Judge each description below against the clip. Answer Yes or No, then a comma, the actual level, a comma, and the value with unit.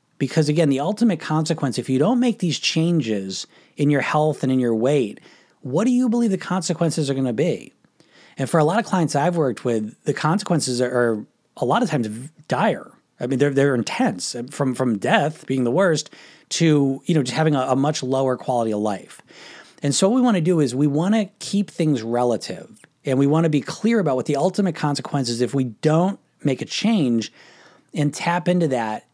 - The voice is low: No, medium, 145 Hz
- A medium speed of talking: No, fast, 215 wpm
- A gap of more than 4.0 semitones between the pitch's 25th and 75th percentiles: Yes, average, 4.8 semitones